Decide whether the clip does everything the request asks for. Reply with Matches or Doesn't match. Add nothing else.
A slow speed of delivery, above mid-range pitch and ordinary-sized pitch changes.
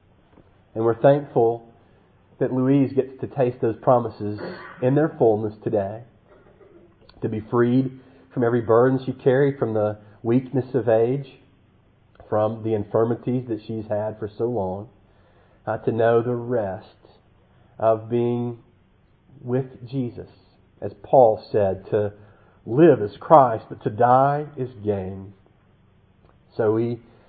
Doesn't match